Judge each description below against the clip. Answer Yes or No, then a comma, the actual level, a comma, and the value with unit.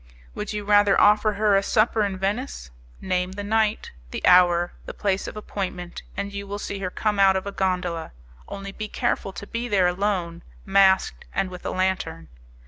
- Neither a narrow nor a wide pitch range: No, narrow, 2.1 semitones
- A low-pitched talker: No, high, 195 Hz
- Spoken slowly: No, average, 190 wpm